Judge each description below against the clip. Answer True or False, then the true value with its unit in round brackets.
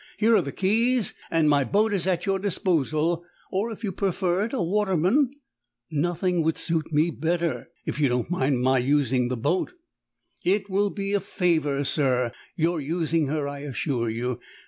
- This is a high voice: False (165 Hz)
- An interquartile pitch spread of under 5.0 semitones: False (5.3 semitones)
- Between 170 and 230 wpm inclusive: True (180 wpm)